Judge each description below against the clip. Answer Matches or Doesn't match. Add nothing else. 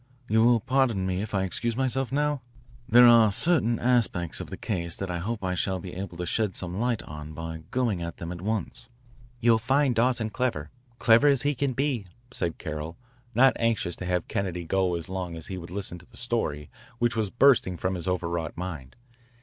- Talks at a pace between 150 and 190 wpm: Doesn't match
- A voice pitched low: Matches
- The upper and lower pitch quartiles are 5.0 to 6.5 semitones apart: Matches